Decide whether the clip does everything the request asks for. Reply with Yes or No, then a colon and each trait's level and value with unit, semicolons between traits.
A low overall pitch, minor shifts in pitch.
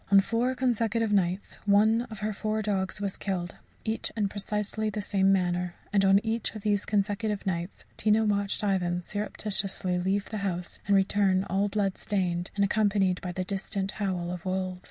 No: high, 200 Hz; narrow, 2.0 semitones